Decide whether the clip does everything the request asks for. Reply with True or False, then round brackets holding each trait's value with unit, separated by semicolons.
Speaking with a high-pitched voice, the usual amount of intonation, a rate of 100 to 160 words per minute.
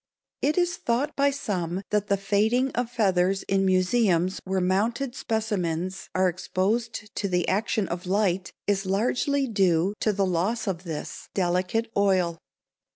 True (195 Hz; 3.6 semitones; 150 wpm)